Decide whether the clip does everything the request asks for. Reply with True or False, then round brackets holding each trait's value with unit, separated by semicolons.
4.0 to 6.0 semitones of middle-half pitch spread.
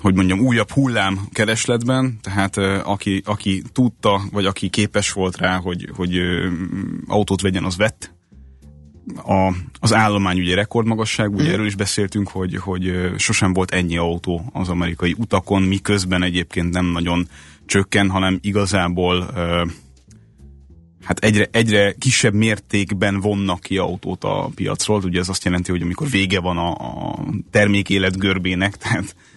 False (2.5 semitones)